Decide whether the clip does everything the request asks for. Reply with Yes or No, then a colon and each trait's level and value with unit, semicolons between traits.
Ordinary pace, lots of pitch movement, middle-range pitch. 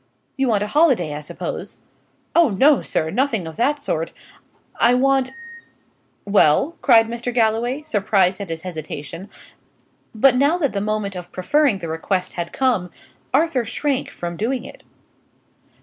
No: average, 150 wpm; wide, 6.7 semitones; high, 225 Hz